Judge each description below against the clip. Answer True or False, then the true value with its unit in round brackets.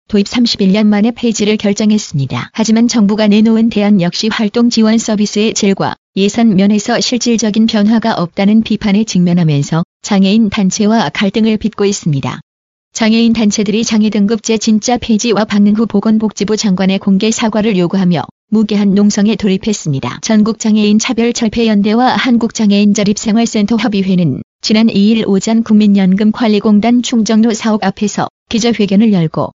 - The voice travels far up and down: False (1.8 semitones)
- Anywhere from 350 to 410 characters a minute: True (365 characters per minute)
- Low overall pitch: False (215 Hz)